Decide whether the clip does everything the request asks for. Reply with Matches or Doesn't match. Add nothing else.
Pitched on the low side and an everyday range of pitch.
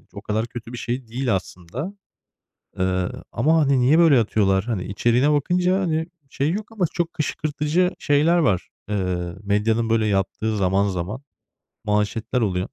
Doesn't match